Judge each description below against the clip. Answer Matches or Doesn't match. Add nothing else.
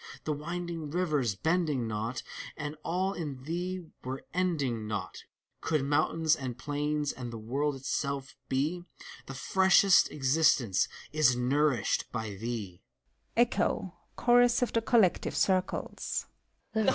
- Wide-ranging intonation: Doesn't match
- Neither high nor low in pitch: Matches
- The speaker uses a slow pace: Matches